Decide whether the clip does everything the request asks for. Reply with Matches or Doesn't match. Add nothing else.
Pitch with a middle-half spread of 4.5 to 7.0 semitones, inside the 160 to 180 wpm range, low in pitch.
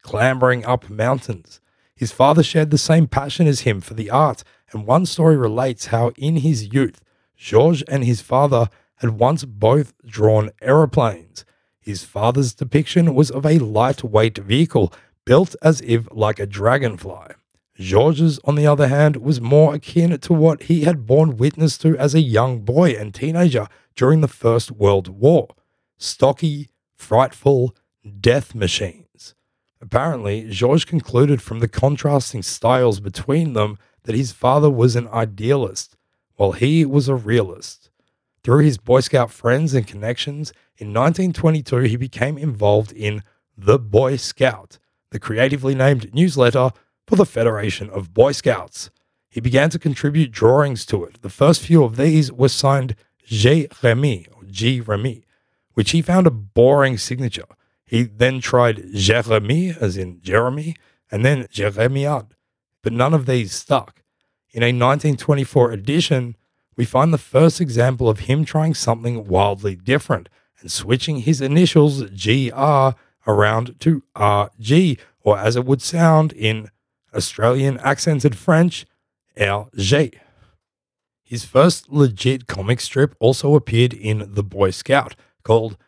Doesn't match